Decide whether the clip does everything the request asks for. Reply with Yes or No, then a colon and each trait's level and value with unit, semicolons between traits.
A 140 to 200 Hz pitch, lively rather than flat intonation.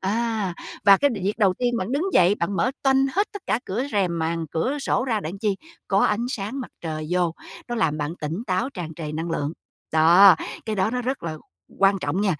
Yes: high, 195 Hz; wide, 5.9 semitones